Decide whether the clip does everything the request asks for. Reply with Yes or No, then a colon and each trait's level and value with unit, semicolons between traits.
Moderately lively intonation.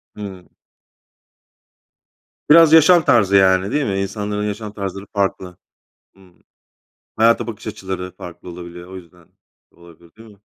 Yes: average, 3.0 semitones